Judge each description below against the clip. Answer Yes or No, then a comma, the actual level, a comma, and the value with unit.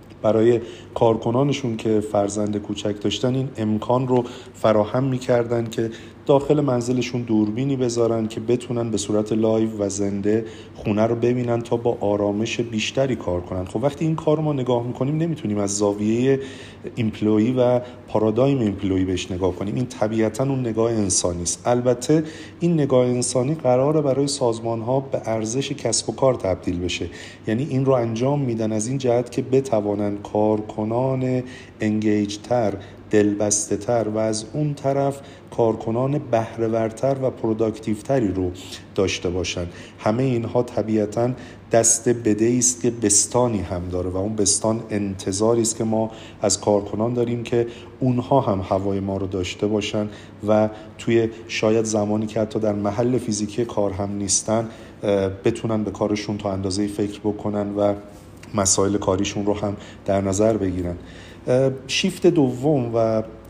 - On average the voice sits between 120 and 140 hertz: No, low, 110 Hz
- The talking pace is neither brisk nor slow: Yes, average, 145 wpm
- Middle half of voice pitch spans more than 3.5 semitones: No, average, 3.0 semitones